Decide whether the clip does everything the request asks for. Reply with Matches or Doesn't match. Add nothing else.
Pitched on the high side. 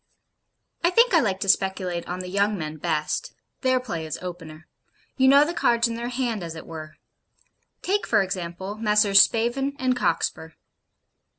Matches